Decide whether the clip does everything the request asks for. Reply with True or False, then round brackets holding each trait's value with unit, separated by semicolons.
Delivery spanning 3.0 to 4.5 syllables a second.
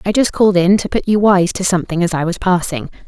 False (6.3 syllables/s)